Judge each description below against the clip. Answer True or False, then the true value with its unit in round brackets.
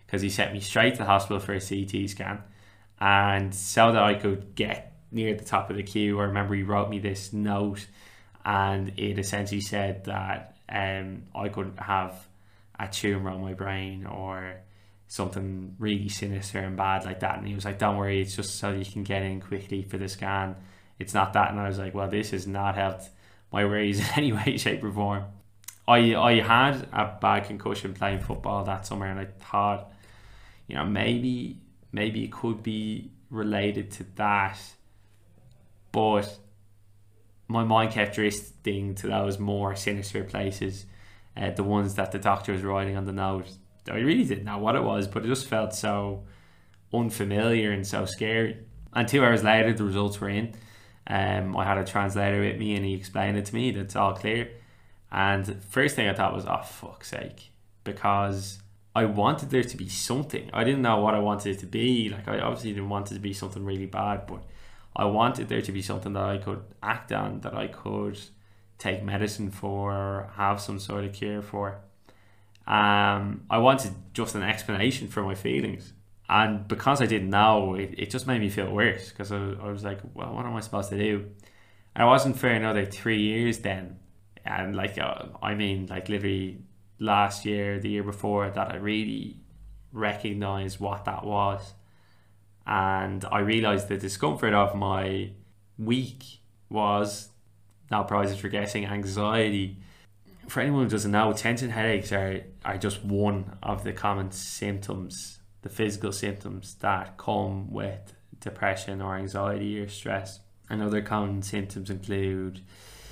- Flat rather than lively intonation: True (1.3 semitones)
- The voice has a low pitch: True (100 Hz)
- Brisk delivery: False (180 wpm)